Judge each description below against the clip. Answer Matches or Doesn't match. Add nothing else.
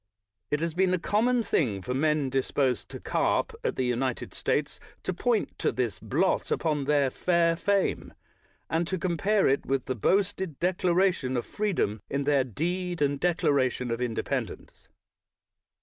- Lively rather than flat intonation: Matches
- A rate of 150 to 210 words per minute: Matches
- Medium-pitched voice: Matches